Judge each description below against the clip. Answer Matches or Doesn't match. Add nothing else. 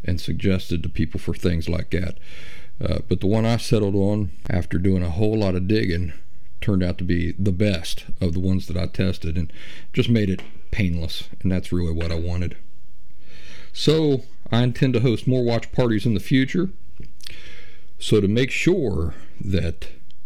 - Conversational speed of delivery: Matches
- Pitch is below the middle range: Matches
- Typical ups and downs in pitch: Matches